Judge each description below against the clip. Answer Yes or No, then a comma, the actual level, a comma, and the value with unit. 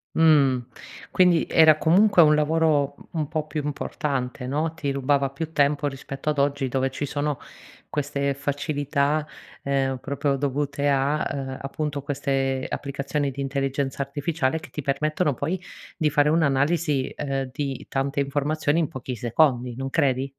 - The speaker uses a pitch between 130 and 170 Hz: Yes, medium, 140 Hz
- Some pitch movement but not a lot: No, narrow, 1.9 semitones